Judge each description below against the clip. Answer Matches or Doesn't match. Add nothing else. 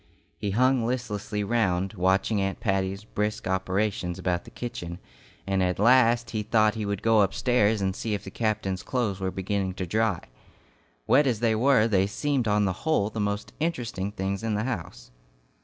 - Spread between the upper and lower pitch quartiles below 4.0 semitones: Matches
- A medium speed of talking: Matches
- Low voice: Matches